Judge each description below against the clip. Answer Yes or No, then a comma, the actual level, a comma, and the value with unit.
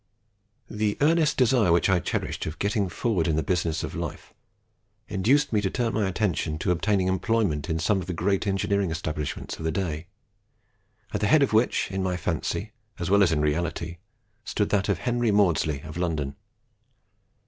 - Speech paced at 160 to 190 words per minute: Yes, average, 185 wpm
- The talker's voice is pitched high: No, very low, 95 Hz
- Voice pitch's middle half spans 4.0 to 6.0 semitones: Yes, average, 4.4 semitones